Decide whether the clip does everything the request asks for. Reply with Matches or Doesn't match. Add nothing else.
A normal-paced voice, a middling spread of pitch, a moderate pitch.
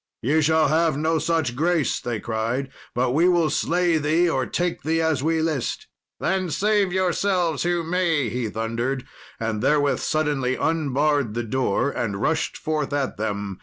Matches